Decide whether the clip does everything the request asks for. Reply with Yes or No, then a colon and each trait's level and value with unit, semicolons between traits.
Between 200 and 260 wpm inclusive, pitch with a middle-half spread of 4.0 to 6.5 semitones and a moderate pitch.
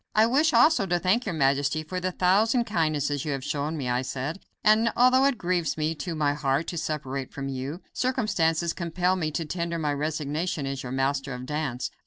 Yes: fast, 205 wpm; average, 4.6 semitones; medium, 155 Hz